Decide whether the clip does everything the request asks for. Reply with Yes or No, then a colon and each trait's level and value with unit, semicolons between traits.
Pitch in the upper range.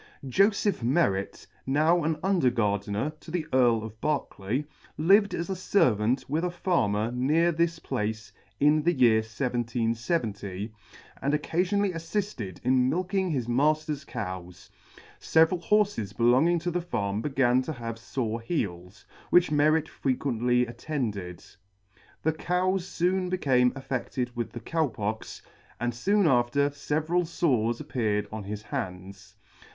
No: low, 130 Hz